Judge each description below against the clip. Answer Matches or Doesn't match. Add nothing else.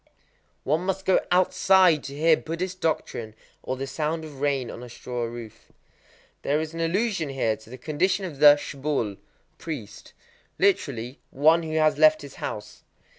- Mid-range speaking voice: Matches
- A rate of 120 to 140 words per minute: Doesn't match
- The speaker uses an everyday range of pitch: Matches